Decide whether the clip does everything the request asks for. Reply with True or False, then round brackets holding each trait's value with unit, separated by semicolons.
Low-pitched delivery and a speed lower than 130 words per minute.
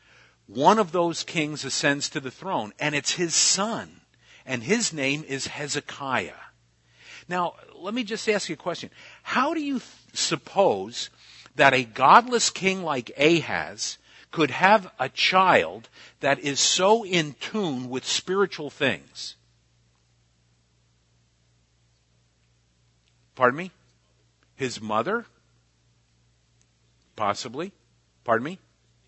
True (130 Hz; 115 wpm)